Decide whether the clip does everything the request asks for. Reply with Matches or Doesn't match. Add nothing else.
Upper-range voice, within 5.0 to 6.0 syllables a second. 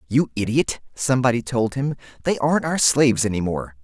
Doesn't match